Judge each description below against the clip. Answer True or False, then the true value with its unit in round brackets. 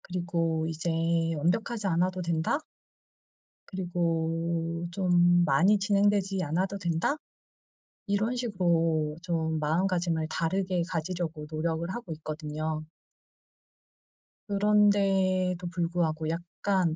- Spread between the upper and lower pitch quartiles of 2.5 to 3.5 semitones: True (2.8 semitones)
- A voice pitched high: False (175 Hz)